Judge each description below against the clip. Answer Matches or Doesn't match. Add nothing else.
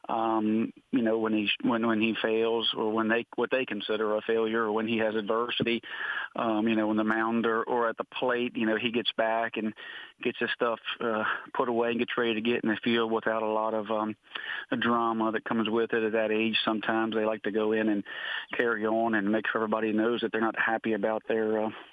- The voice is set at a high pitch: Doesn't match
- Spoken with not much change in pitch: Matches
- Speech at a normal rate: Doesn't match